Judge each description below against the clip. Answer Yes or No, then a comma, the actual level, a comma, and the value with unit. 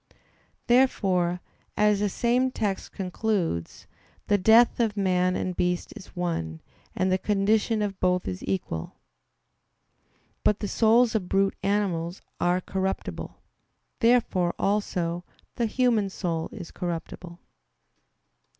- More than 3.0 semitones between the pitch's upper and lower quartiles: Yes, average, 3.4 semitones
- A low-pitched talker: No, high, 195 Hz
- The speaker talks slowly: Yes, slow, 115 wpm